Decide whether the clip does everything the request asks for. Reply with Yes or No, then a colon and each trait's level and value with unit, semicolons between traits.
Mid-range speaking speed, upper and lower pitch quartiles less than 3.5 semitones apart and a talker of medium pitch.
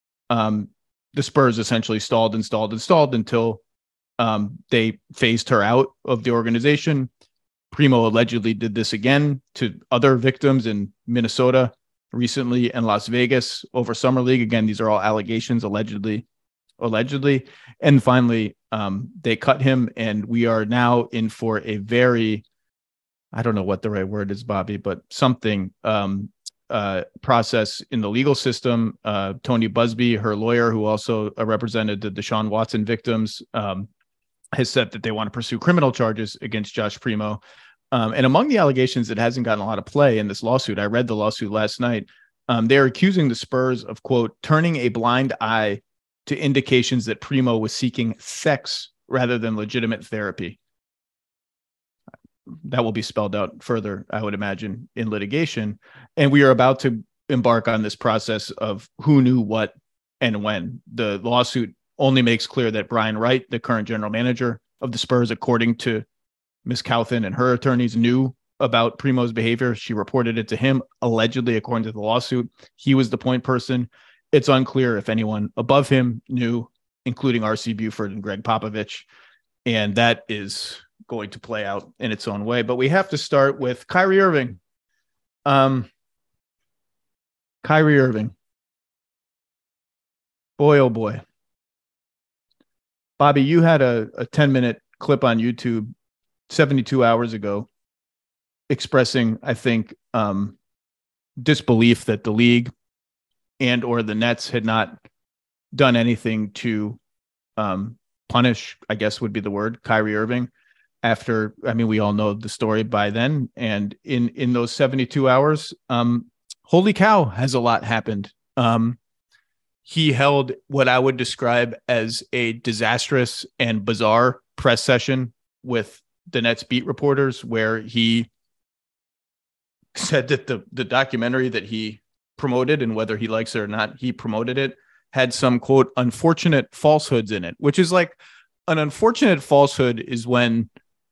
No: average, 155 wpm; average, 2.9 semitones; low, 115 Hz